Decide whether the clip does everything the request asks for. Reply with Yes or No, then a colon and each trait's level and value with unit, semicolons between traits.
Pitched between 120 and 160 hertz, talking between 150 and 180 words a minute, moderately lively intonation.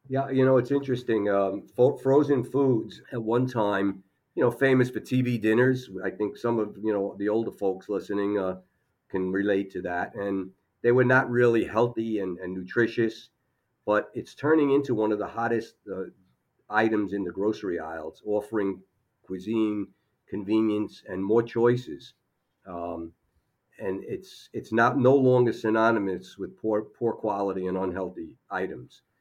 No: low, 110 Hz; average, 160 wpm; average, 3.6 semitones